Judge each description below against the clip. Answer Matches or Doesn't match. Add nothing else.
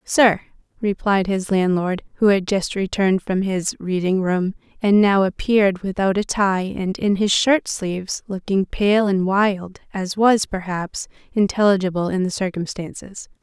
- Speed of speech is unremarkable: Matches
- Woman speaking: Matches